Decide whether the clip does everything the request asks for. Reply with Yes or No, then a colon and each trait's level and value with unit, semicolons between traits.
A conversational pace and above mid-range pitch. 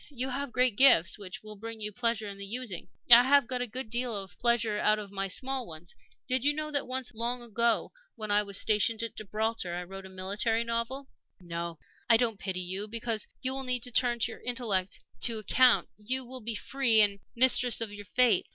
No: fast, 215 wpm; high, 230 Hz